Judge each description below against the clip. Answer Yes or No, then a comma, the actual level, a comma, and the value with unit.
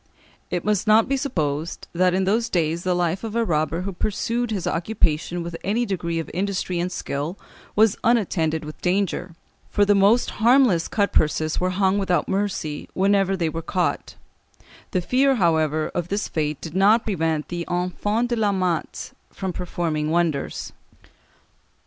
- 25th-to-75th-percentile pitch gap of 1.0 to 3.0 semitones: No, average, 3.8 semitones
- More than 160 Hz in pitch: Yes, medium, 185 Hz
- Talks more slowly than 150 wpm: No, average, 165 wpm